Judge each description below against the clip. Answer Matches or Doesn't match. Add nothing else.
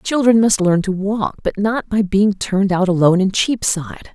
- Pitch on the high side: Matches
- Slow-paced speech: Doesn't match